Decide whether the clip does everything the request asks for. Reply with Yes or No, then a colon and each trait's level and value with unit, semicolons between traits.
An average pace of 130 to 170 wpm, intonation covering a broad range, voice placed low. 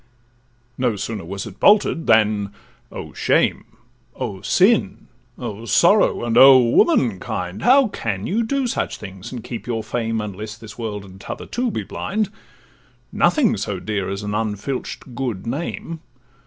Yes: average, 150 wpm; wide, 7.9 semitones; low, 115 Hz